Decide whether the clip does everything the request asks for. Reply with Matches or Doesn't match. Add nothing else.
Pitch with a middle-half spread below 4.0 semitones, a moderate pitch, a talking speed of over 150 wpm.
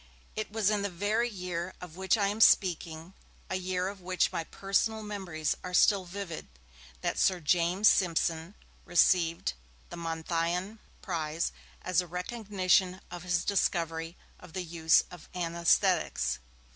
Doesn't match